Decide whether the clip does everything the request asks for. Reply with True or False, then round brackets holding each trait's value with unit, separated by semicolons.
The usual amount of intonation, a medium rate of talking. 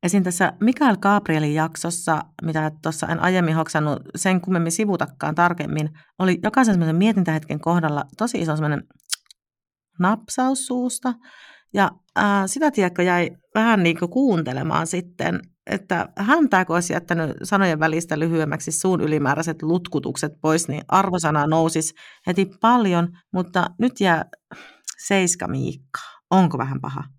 True (3.9 semitones; 130 wpm)